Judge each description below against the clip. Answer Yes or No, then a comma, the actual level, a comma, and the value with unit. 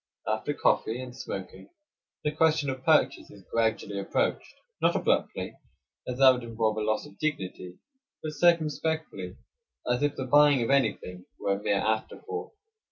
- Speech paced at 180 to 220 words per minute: No, average, 155 wpm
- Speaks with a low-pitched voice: Yes, low, 125 Hz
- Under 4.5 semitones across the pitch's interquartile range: No, wide, 5.6 semitones